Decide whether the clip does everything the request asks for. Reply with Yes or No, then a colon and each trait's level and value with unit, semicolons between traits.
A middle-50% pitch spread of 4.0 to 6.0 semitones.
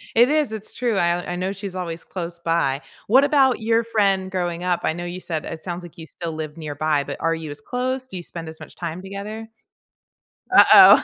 Yes: average, 4.6 semitones